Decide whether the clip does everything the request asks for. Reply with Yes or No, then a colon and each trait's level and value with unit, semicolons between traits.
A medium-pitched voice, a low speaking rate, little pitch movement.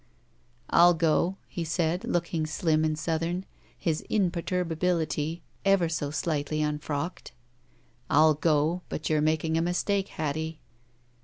Yes: medium, 160 Hz; slow, 125 wpm; narrow, 2.2 semitones